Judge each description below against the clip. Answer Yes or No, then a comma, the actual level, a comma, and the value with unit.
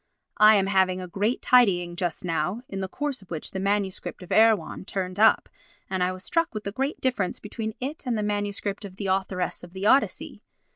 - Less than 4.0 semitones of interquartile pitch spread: Yes, average, 2.9 semitones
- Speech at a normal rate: No, fast, 210 wpm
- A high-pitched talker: Yes, high, 200 Hz